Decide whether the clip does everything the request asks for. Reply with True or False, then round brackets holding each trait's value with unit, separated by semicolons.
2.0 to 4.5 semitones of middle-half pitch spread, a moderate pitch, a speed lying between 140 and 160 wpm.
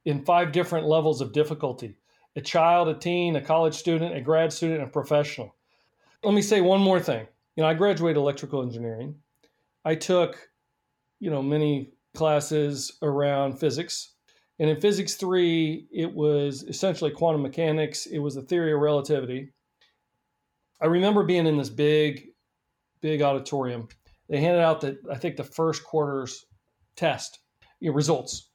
True (2.7 semitones; 155 Hz; 150 wpm)